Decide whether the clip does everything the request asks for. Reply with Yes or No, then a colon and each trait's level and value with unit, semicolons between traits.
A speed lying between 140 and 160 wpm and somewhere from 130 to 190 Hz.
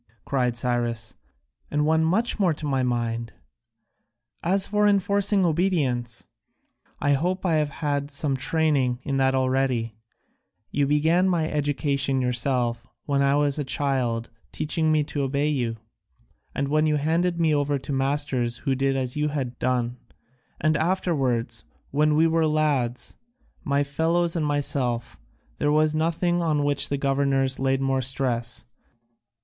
Yes: average, 150 wpm; medium, 140 Hz